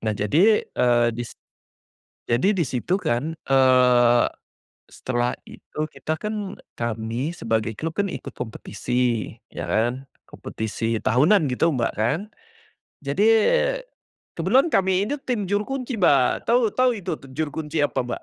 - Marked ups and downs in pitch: Yes, wide, 8.1 semitones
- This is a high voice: No, low, 135 Hz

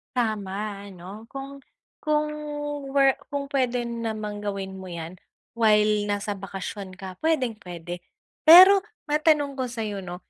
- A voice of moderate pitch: No, high, 215 Hz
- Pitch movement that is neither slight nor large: No, wide, 5.8 semitones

